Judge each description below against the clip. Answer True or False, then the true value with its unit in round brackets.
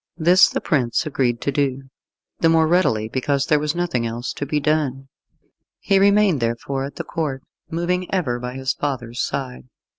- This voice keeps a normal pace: True (175 wpm)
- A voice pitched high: False (140 Hz)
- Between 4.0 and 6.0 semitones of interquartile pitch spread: True (4.5 semitones)